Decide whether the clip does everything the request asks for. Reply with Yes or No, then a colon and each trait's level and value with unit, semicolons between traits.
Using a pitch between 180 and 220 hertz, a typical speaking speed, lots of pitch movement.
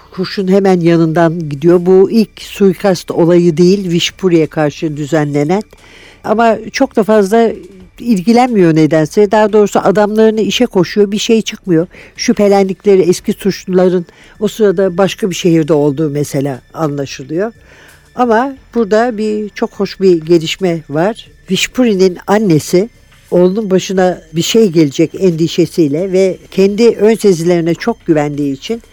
No: high, 190 Hz; average, 125 wpm; average, 4.1 semitones